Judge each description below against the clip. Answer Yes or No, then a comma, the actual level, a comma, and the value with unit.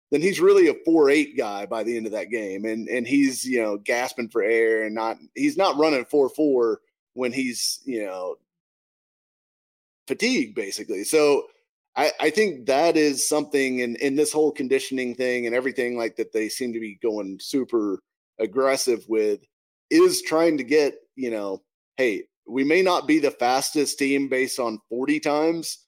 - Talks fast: No, average, 175 wpm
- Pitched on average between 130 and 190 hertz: Yes, medium, 140 Hz